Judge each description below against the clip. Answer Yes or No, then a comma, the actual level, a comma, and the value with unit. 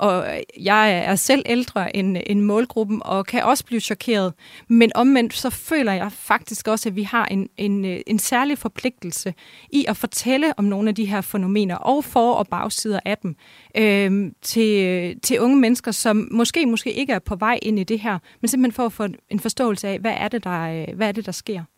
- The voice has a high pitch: Yes, high, 215 Hz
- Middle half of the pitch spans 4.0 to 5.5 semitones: No, average, 3.0 semitones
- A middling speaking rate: Yes, average, 210 wpm